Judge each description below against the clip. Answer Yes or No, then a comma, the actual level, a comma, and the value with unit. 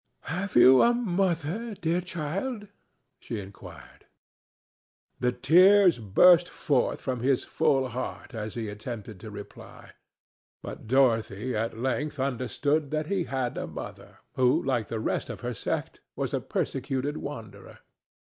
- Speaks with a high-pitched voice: No, low, 135 Hz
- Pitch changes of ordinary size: No, wide, 6.5 semitones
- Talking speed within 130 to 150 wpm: Yes, slow, 135 wpm